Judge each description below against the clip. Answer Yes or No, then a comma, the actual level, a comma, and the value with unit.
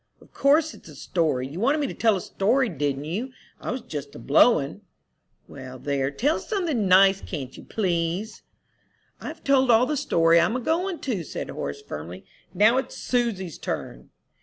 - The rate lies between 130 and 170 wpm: No, average, 180 wpm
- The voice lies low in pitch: No, high, 195 Hz